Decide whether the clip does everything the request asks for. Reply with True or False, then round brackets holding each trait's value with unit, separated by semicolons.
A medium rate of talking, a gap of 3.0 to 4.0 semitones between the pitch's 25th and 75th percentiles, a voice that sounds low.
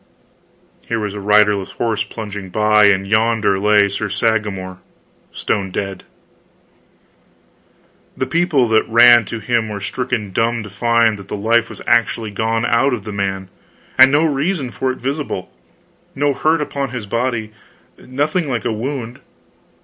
True (150 wpm; 3.5 semitones; 110 Hz)